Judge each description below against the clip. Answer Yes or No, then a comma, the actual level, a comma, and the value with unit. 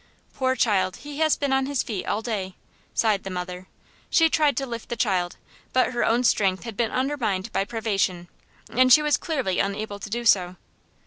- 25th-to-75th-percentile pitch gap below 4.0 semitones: No, average, 5.2 semitones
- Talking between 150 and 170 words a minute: No, average, 195 wpm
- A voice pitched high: Yes, high, 225 Hz